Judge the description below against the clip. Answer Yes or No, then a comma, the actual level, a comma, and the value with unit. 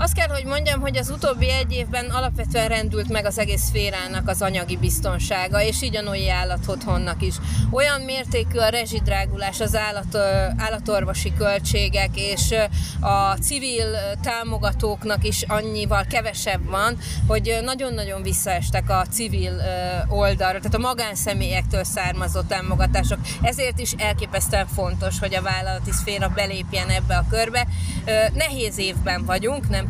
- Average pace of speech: Yes, average, 130 wpm